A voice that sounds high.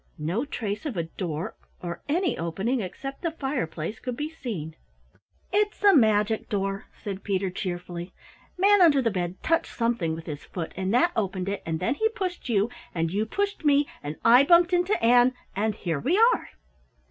Yes: high, 220 Hz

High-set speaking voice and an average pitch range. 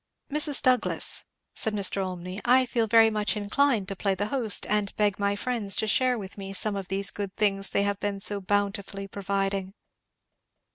No: high, 205 Hz; narrow, 1.9 semitones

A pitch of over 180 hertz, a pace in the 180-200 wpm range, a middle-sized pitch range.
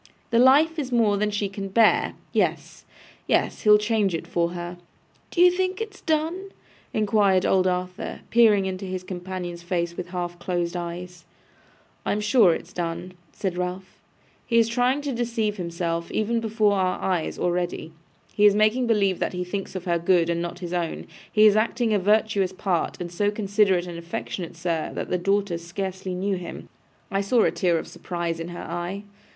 Yes: high, 190 Hz; average, 185 wpm; average, 3.5 semitones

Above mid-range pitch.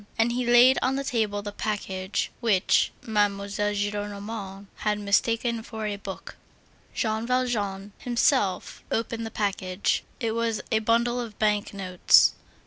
Yes: high, 215 Hz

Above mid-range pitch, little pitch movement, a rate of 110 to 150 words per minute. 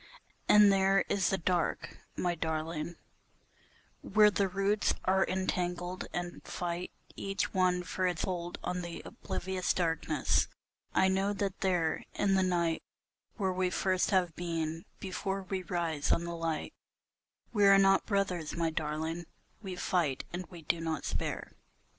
No: medium, 180 Hz; narrow, 2.3 semitones; average, 145 wpm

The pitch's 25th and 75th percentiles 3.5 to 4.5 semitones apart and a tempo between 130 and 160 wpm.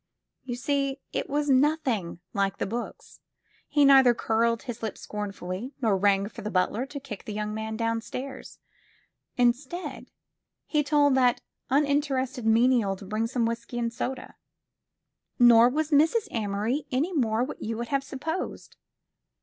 Yes: average, 4.0 semitones; average, 150 wpm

